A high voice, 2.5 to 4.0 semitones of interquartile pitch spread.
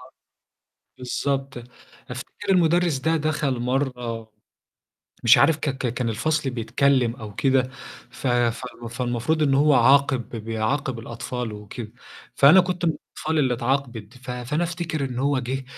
No: low, 130 Hz; average, 3.3 semitones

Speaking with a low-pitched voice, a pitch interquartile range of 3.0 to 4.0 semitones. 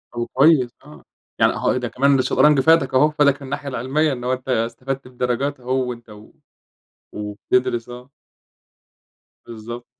No: low, 125 Hz; narrow, 2.6 semitones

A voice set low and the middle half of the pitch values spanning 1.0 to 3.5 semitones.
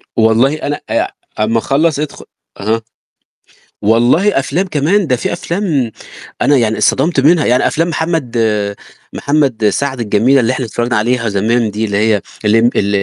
No: low, 125 Hz; average, 5.1 semitones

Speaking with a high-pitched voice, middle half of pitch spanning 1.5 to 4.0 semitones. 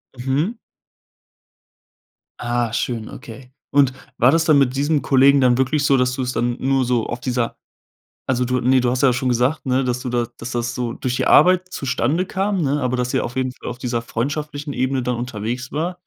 No: low, 130 Hz; narrow, 2.4 semitones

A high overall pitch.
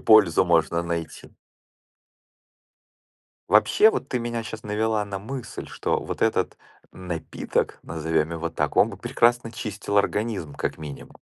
No: low, 100 Hz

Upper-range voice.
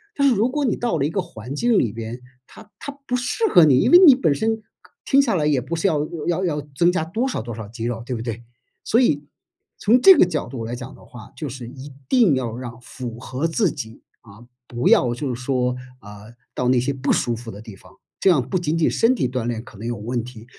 No: low, 130 Hz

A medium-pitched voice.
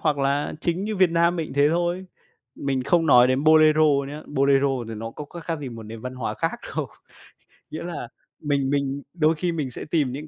Yes: medium, 150 Hz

